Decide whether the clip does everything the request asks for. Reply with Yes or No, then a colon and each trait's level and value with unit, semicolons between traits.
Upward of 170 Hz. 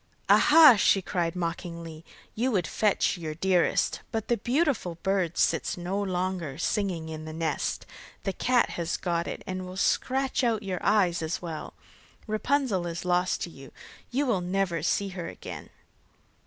Yes: medium, 185 Hz